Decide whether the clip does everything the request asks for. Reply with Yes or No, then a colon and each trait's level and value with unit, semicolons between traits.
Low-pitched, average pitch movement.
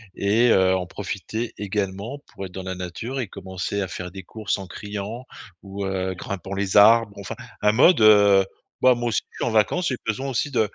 Yes: low, 100 Hz; average, 3.0 semitones